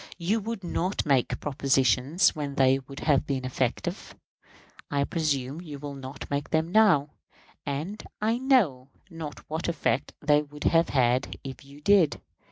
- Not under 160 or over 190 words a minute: No, average, 150 wpm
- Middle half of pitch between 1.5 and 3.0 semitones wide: No, average, 3.8 semitones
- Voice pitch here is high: No, medium, 145 Hz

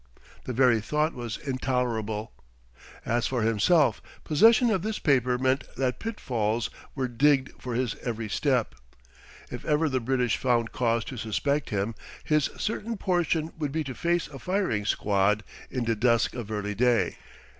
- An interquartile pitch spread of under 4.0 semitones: No, average, 4.7 semitones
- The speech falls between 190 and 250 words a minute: No, average, 155 wpm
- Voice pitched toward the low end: Yes, low, 125 Hz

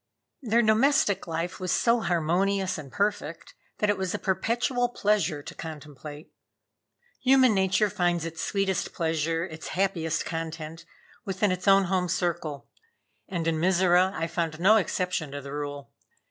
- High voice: No, medium, 180 Hz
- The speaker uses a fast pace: No, average, 145 wpm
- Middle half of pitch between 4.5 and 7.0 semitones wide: No, average, 3.4 semitones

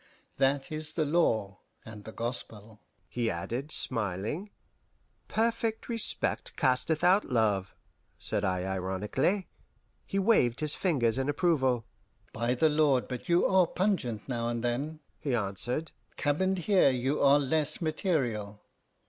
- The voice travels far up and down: Yes, wide, 6.0 semitones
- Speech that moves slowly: Yes, slow, 130 wpm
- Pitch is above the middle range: No, low, 135 Hz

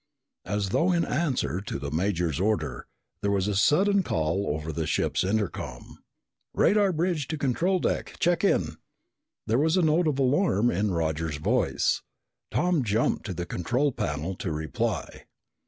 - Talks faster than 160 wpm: No, average, 155 wpm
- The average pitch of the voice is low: Yes, low, 105 Hz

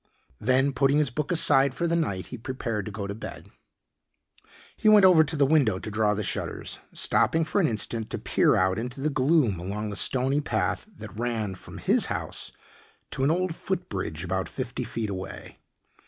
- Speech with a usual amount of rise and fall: No, wide, 6.4 semitones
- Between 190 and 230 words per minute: Yes, average, 195 wpm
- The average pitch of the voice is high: No, low, 125 Hz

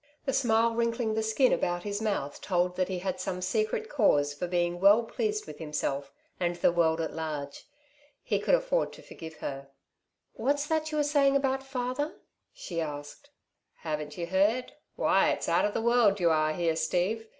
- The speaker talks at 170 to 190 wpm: Yes, average, 185 wpm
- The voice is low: No, high, 195 Hz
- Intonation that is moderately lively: No, wide, 7.1 semitones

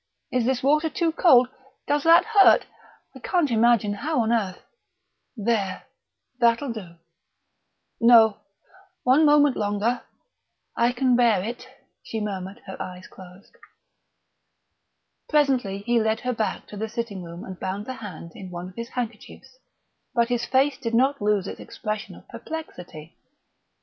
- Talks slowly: No, average, 150 wpm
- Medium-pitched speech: No, high, 230 Hz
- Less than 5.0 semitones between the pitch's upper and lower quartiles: Yes, average, 4.3 semitones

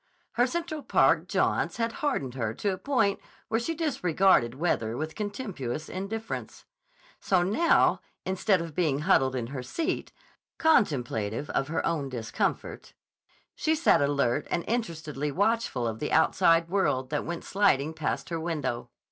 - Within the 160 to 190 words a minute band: No, average, 150 wpm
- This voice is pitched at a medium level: Yes, medium, 165 Hz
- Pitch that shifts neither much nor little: No, wide, 7.7 semitones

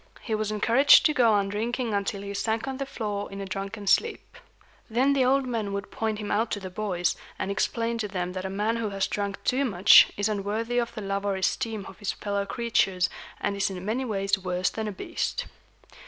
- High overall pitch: Yes, high, 205 Hz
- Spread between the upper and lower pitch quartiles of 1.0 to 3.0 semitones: Yes, average, 2.7 semitones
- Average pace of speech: No, fast, 225 wpm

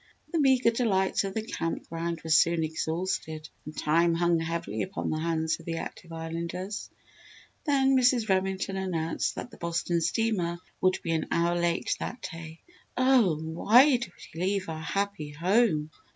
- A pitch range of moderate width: Yes, average, 3.7 semitones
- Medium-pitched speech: Yes, medium, 170 Hz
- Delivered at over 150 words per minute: Yes, average, 165 wpm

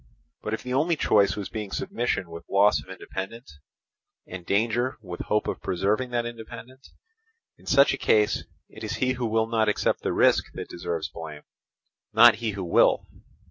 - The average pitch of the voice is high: No, low, 110 Hz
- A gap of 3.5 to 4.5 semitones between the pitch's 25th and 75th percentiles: Yes, average, 3.9 semitones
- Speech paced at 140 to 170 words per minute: No, average, 180 wpm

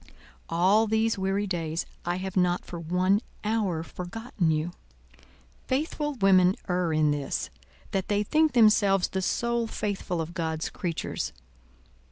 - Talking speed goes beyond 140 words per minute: No, slow, 135 wpm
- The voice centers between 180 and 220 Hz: Yes, high, 190 Hz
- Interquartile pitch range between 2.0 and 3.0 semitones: No, average, 3.8 semitones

